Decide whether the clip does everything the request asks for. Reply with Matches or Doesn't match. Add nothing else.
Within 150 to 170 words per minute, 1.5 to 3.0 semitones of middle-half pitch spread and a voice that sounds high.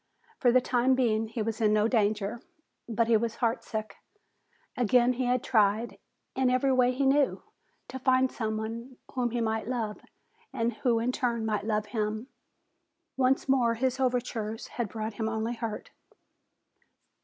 Matches